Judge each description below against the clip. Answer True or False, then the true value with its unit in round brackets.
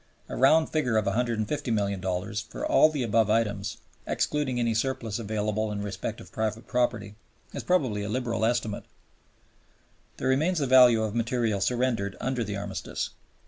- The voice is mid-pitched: False (115 Hz)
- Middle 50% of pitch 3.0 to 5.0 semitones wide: True (3.5 semitones)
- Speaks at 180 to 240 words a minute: False (150 wpm)